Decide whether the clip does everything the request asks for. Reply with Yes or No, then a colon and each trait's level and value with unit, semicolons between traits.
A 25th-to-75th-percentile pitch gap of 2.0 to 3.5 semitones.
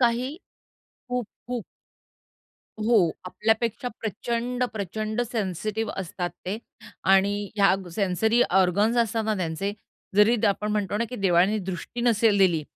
Yes: average, 3.2 semitones